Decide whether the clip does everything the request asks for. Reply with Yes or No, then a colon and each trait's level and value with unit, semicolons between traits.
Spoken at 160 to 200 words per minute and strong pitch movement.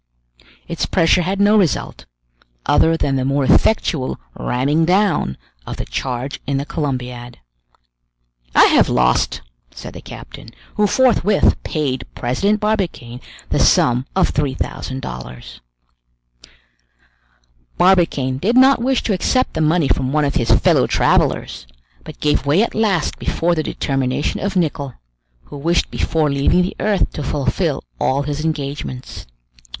No: average, 140 wpm; wide, 5.9 semitones